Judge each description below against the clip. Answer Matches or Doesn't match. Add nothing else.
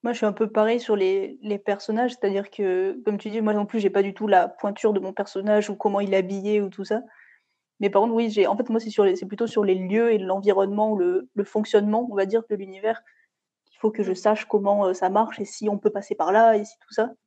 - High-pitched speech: Matches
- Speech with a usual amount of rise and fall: Doesn't match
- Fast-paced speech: Matches